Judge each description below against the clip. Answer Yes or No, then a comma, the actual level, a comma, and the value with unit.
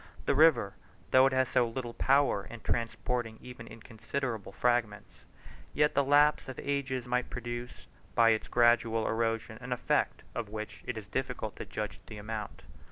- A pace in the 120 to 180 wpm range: Yes, average, 165 wpm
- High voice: No, low, 120 Hz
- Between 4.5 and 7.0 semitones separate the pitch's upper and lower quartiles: No, average, 2.8 semitones